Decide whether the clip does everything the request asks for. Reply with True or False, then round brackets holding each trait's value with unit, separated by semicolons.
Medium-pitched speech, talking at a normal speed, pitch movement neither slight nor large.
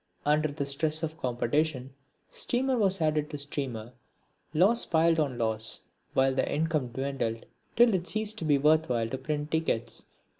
True (150 Hz; 160 wpm; 3.5 semitones)